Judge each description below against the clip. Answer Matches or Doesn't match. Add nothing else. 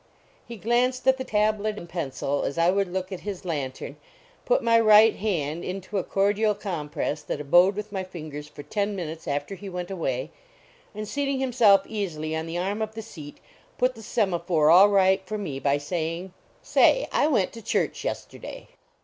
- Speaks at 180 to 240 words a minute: Matches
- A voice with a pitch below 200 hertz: Matches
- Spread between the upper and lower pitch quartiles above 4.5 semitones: Matches